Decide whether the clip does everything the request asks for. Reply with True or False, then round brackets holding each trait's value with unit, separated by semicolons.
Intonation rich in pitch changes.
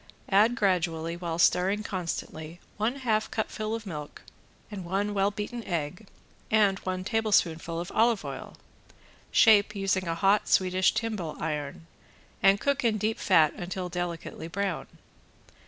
False (3.9 semitones)